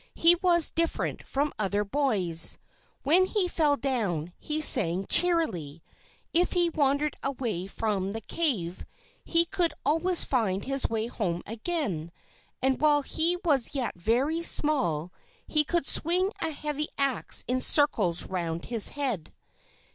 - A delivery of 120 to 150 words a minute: Yes, average, 140 wpm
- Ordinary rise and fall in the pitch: No, wide, 8.3 semitones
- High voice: Yes, very high, 275 Hz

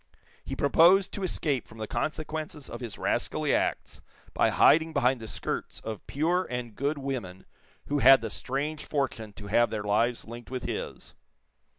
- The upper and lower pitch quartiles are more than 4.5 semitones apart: Yes, average, 5.2 semitones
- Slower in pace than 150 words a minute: No, average, 170 wpm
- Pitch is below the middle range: Yes, low, 130 Hz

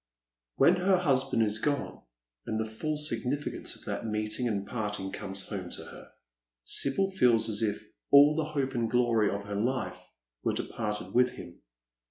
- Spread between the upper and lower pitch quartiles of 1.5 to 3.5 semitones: No, average, 4.8 semitones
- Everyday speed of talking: Yes, average, 170 wpm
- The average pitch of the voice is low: Yes, low, 115 Hz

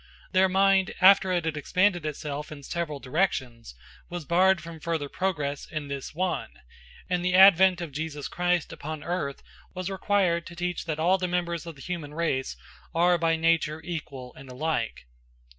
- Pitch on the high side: No, medium, 170 Hz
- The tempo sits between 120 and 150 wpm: No, average, 170 wpm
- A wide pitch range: No, average, 3.4 semitones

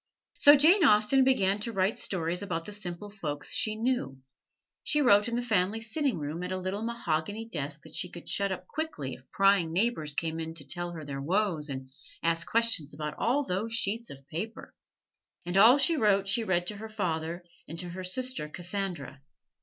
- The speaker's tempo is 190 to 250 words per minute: Yes, average, 195 wpm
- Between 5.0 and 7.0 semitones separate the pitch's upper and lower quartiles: Yes, wide, 5.5 semitones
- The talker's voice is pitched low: No, high, 190 Hz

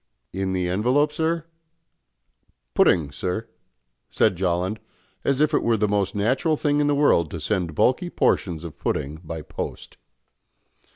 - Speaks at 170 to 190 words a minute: No, average, 150 wpm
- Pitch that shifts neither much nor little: No, wide, 8.6 semitones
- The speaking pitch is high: No, low, 100 Hz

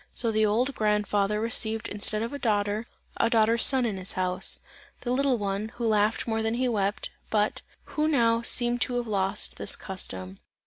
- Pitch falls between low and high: No, high, 220 Hz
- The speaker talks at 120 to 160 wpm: No, average, 185 wpm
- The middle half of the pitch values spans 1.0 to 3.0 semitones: Yes, narrow, 2.6 semitones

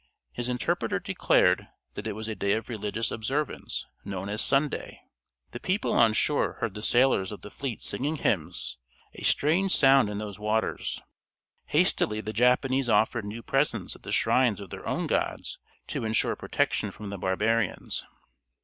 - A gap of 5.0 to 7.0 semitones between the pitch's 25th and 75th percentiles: No, average, 3.9 semitones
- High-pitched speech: No, low, 110 Hz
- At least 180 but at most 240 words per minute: No, average, 165 wpm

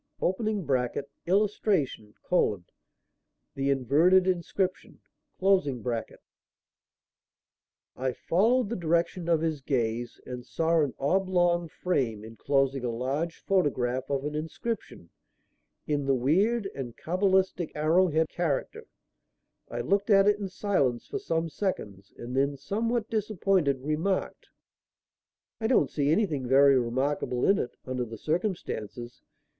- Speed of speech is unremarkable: No, slow, 115 wpm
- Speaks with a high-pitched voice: No, medium, 155 Hz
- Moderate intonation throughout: No, wide, 6.3 semitones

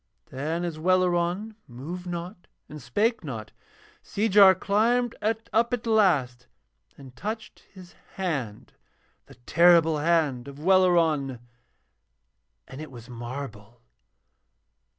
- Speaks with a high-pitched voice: No, medium, 170 Hz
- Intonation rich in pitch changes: Yes, wide, 6.2 semitones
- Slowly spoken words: Yes, slow, 105 wpm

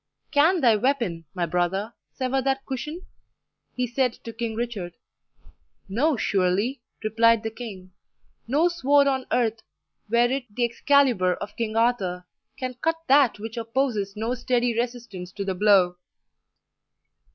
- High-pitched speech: Yes, high, 235 Hz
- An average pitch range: Yes, average, 4.3 semitones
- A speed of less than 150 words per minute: Yes, average, 140 wpm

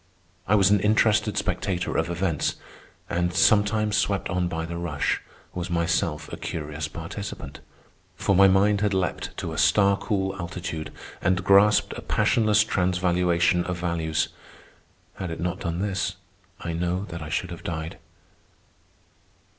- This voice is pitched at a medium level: No, very low, 90 Hz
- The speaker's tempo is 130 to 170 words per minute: Yes, average, 145 wpm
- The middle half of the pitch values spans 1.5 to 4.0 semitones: Yes, average, 2.8 semitones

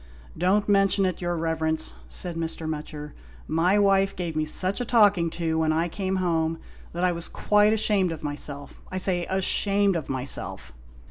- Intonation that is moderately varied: Yes, average, 3.4 semitones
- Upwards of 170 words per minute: Yes, average, 185 wpm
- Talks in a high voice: No, medium, 175 Hz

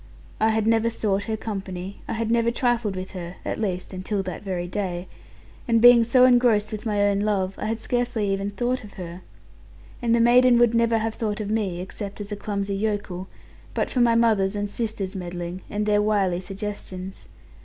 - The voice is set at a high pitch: Yes, high, 210 Hz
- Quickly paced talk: No, average, 195 wpm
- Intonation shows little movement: No, average, 3.0 semitones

